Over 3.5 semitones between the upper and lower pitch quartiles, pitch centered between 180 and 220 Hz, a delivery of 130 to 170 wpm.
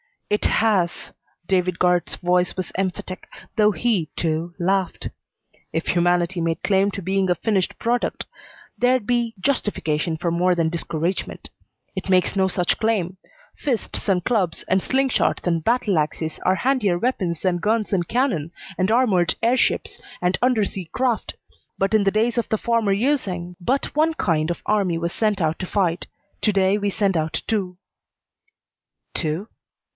Yes: average, 4.0 semitones; high, 190 Hz; average, 160 wpm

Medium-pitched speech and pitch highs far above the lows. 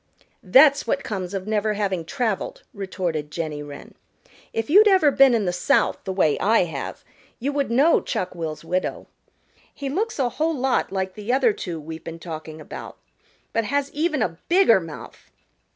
No: high, 205 Hz; wide, 8.4 semitones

